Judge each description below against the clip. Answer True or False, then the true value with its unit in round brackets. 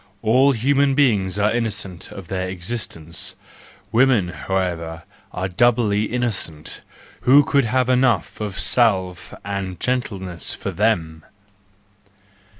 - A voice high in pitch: False (105 Hz)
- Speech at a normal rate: False (110 wpm)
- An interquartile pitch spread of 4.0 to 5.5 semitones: True (4.9 semitones)